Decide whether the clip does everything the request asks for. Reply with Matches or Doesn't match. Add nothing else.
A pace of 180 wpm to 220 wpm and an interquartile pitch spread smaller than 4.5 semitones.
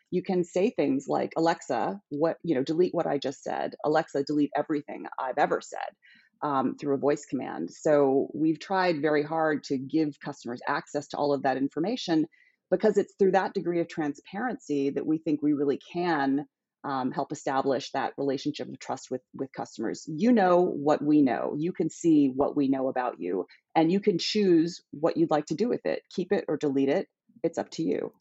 Matches